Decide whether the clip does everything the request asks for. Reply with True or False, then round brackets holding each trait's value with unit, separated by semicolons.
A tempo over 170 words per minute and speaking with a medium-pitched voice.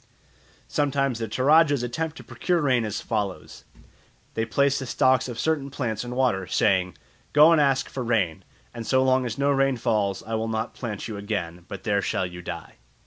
False (195 wpm; 120 Hz)